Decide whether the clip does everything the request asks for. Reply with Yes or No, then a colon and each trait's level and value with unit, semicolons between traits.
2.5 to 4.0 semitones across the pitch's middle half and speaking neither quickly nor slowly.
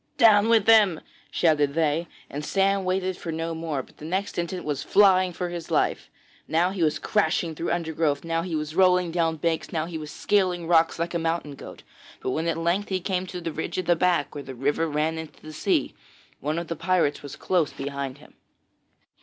No: average, 2.8 semitones; fast, 210 wpm